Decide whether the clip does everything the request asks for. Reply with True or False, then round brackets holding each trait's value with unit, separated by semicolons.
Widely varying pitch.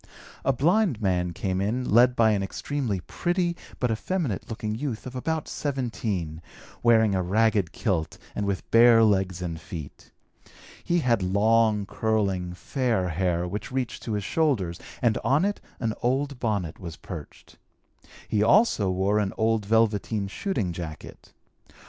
False (4.8 semitones)